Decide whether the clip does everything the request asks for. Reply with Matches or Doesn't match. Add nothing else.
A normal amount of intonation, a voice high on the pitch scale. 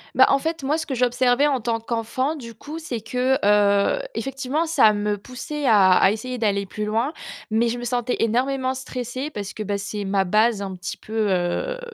Matches